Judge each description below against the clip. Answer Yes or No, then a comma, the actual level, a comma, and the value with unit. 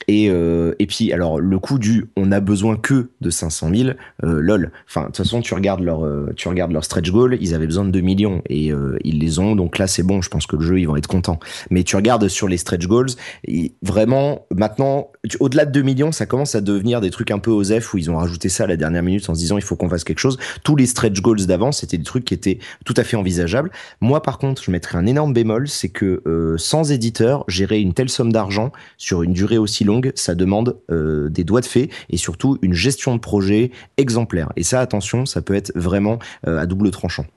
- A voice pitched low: Yes, low, 100 Hz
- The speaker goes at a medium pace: No, fast, 255 wpm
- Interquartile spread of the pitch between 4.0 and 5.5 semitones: Yes, average, 5.2 semitones